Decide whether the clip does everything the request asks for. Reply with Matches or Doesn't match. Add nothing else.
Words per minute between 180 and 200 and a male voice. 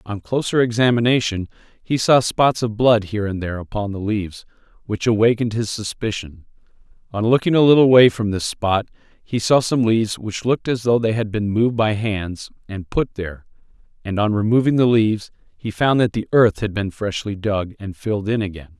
Matches